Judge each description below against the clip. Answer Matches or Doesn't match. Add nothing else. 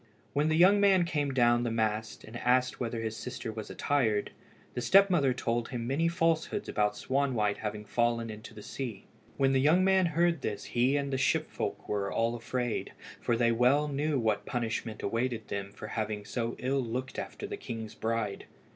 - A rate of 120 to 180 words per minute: Doesn't match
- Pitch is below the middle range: Matches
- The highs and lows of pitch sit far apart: Doesn't match